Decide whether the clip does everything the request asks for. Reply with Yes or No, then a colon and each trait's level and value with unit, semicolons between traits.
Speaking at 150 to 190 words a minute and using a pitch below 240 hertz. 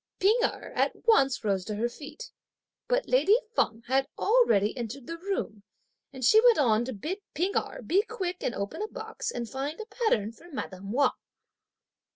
No: average, 185 wpm; very high, 280 Hz